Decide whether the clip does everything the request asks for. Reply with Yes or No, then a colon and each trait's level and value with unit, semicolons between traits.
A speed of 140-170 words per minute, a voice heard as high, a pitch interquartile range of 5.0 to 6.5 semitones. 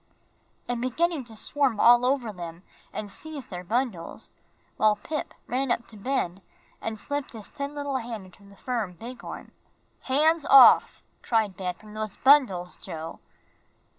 Yes: average, 155 wpm; high, 230 Hz; average, 5.3 semitones